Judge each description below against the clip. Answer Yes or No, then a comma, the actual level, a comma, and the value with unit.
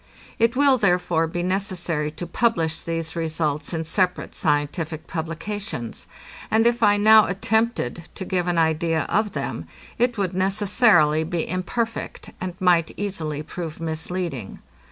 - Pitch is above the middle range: No, medium, 175 Hz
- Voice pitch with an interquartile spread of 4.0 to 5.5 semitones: Yes, average, 4.3 semitones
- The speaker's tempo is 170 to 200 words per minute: No, slow, 135 wpm